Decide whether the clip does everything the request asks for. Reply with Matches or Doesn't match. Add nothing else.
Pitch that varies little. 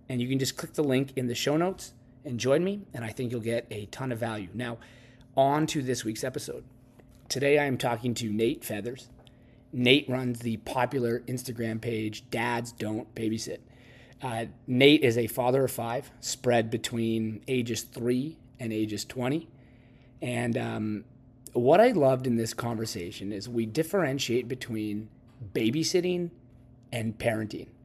Matches